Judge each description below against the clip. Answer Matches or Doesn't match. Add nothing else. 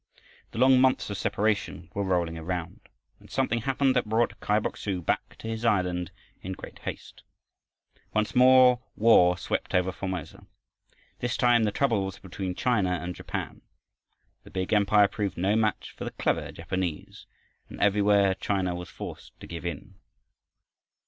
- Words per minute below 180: Matches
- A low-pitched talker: Matches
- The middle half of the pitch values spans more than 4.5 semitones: Doesn't match